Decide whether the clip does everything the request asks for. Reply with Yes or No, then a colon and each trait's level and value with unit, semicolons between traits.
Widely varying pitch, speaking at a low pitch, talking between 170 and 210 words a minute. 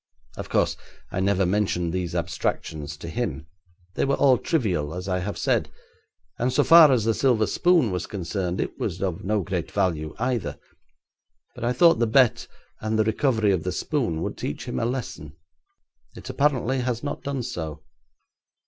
Yes: wide, 6.0 semitones; low, 105 Hz; average, 175 wpm